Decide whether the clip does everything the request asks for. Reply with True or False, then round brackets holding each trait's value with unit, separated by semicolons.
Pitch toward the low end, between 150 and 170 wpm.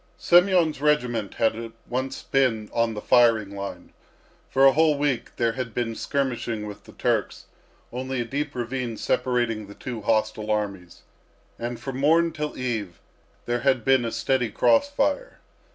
True (120 Hz; 155 wpm)